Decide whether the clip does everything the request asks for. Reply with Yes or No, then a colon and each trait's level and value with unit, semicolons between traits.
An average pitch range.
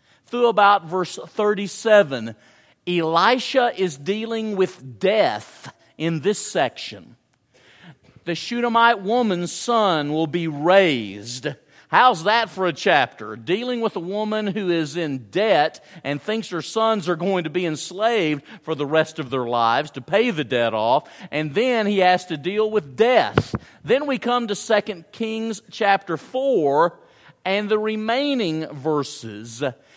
No: wide, 6.2 semitones